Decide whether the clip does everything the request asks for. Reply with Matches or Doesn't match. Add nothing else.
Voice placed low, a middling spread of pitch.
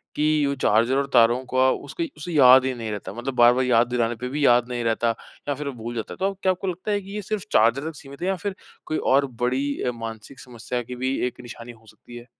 Matches